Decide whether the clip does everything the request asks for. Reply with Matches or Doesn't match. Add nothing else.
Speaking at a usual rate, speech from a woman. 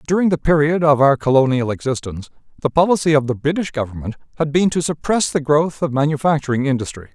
Doesn't match